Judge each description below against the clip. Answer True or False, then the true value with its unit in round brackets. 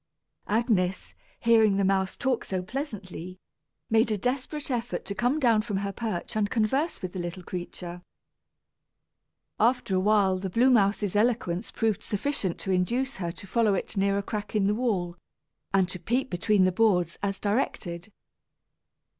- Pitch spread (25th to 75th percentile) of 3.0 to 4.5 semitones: True (3.9 semitones)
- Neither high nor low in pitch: False (205 Hz)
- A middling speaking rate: True (165 wpm)